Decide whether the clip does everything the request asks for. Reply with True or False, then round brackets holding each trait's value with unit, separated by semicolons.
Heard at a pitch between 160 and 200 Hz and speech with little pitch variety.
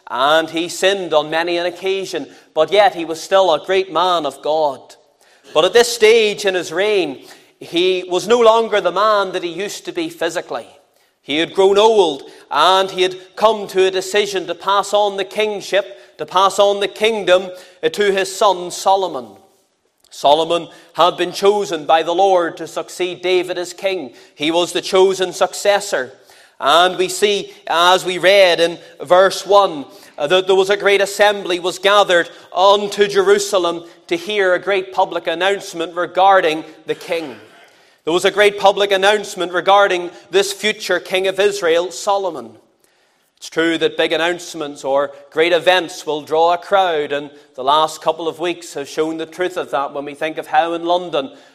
False (185 Hz; 3.1 semitones)